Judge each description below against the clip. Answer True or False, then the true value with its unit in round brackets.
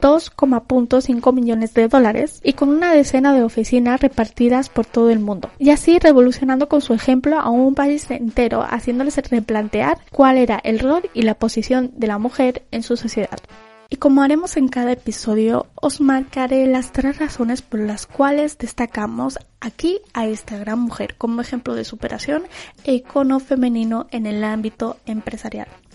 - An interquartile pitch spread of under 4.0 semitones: True (3.4 semitones)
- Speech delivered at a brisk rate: False (165 wpm)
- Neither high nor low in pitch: False (250 Hz)